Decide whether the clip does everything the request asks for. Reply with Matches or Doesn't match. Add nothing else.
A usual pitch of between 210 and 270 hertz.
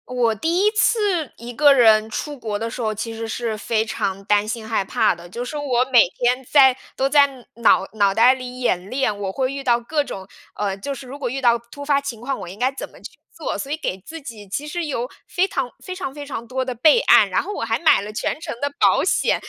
Matches